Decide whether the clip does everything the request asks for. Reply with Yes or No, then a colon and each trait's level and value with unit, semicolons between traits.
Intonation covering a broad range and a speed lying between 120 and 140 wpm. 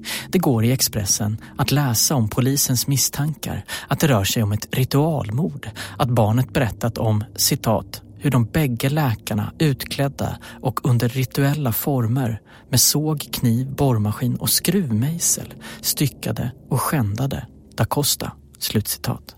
No: average, 4.2 semitones; average, 130 wpm